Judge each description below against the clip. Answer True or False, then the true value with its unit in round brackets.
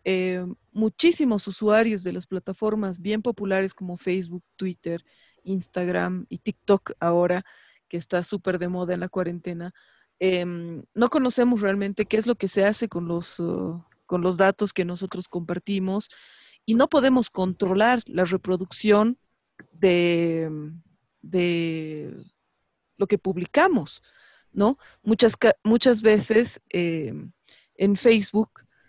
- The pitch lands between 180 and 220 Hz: True (190 Hz)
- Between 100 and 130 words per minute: True (125 wpm)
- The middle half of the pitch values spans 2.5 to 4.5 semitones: True (3.3 semitones)